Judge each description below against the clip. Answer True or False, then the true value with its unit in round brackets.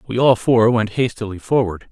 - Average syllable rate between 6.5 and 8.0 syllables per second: False (5.1 syllables/s)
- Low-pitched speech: True (115 Hz)